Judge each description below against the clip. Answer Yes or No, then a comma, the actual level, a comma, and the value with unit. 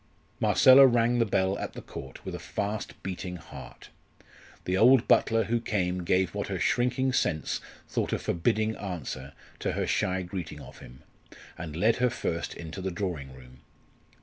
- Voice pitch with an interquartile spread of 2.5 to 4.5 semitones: No, average, 5.1 semitones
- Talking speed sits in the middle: Yes, average, 170 wpm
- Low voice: Yes, very low, 95 Hz